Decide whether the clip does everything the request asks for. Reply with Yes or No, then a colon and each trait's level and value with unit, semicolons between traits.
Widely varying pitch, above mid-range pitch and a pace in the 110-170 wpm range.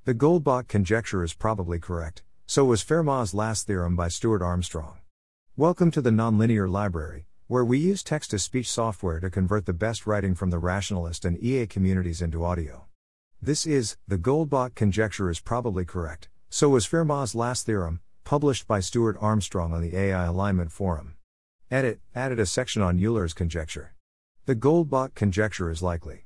No: wide, 5.7 semitones; low, 100 Hz; average, 165 wpm